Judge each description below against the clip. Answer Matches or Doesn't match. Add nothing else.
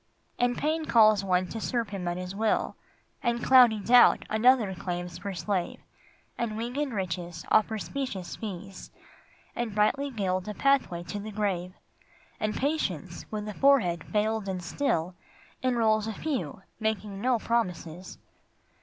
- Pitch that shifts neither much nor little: Matches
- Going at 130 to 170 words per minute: Matches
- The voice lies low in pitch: Doesn't match